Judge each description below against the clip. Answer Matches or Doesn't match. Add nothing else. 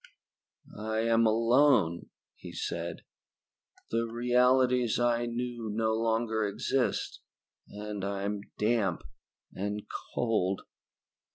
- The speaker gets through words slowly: Matches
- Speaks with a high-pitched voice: Doesn't match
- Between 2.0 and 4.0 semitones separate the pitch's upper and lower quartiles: Matches